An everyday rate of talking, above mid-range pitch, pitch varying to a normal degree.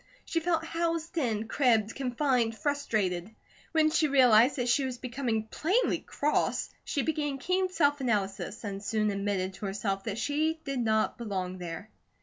No: average, 155 wpm; high, 245 Hz; wide, 5.8 semitones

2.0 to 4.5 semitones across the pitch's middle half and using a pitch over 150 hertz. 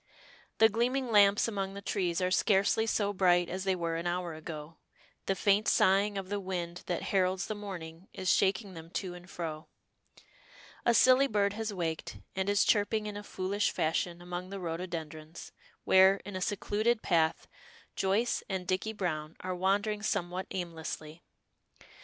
Yes: average, 2.8 semitones; high, 190 Hz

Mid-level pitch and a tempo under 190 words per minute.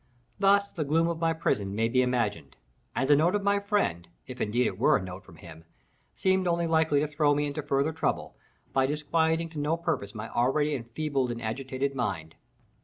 No: medium, 145 Hz; average, 200 wpm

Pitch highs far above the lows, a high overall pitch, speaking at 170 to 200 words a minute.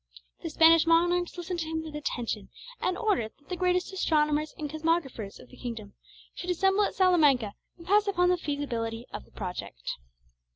Yes: wide, 6.1 semitones; very high, 320 Hz; average, 175 wpm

